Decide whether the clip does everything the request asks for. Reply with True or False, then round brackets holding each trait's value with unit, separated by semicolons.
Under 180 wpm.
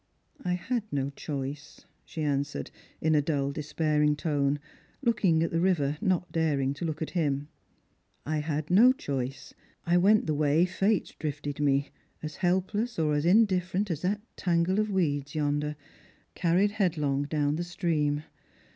True (165 wpm)